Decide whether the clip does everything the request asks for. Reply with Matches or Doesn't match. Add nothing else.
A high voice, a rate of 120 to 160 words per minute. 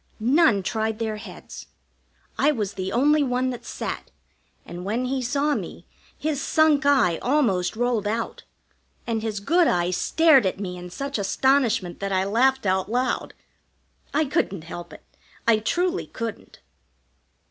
Matches